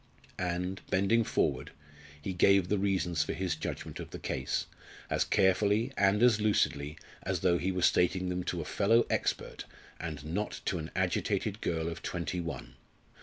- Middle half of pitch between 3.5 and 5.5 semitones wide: No, average, 2.7 semitones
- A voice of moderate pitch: No, very low, 90 Hz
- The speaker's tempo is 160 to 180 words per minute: Yes, average, 170 wpm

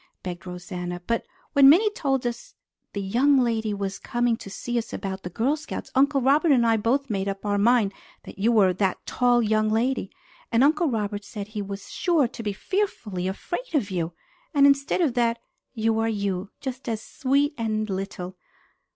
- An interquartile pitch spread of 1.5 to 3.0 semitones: No, average, 5.1 semitones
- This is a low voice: No, high, 225 Hz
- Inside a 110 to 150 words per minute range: No, average, 190 wpm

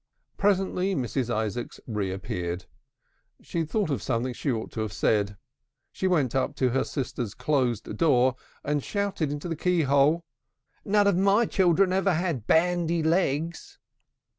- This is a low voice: No, medium, 145 Hz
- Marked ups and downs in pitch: Yes, wide, 6.6 semitones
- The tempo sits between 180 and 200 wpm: No, average, 150 wpm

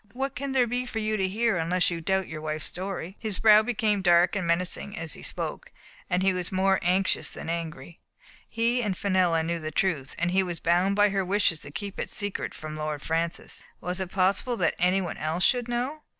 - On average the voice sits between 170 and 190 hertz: Yes, medium, 185 Hz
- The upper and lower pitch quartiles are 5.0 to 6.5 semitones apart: No, average, 3.7 semitones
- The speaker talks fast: Yes, fast, 215 wpm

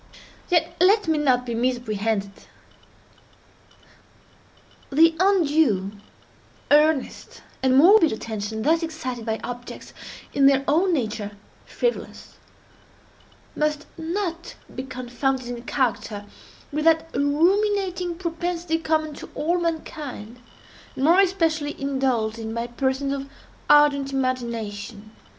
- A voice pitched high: Yes, very high, 280 Hz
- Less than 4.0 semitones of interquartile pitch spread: No, wide, 5.4 semitones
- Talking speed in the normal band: No, slow, 105 wpm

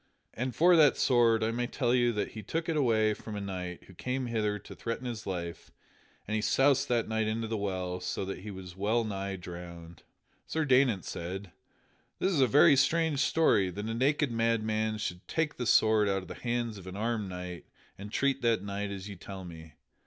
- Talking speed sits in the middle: No, fast, 210 wpm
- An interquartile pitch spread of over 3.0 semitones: Yes, average, 4.2 semitones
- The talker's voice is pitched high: No, low, 110 Hz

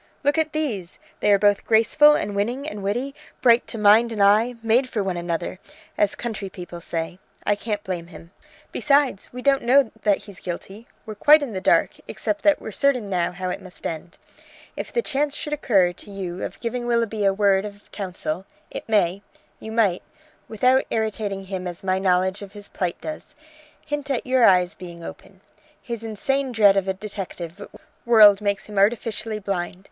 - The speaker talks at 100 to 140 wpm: No, average, 185 wpm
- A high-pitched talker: Yes, high, 205 Hz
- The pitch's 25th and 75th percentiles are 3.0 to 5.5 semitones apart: Yes, average, 4.2 semitones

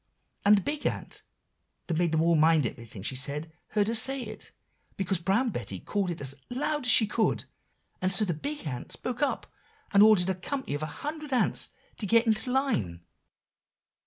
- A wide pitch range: Yes, wide, 7.8 semitones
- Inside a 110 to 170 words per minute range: No, average, 195 wpm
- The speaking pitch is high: Yes, high, 195 Hz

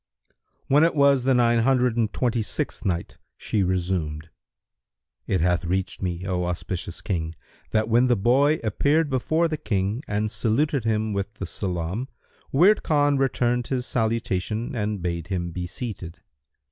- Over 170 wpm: No, average, 155 wpm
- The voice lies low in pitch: Yes, low, 110 Hz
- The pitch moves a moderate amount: No, wide, 5.7 semitones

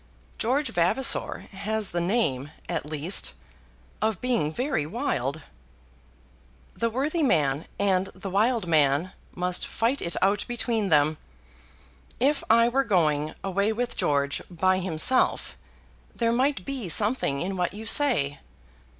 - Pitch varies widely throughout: Yes, wide, 6.9 semitones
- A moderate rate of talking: No, slow, 130 wpm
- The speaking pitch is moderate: No, high, 195 Hz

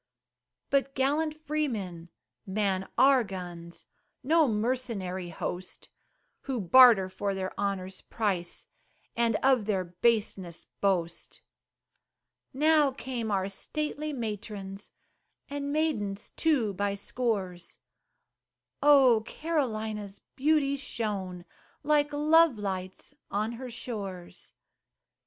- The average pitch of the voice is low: No, high, 215 Hz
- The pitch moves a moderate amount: No, wide, 6.2 semitones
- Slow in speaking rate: Yes, slow, 95 wpm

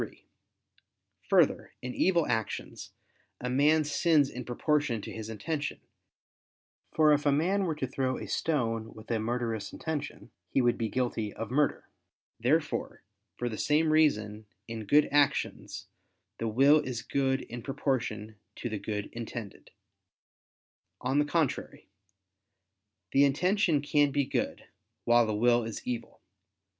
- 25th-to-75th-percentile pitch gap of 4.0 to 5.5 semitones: Yes, average, 4.5 semitones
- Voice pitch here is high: No, low, 130 Hz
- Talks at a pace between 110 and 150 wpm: Yes, average, 140 wpm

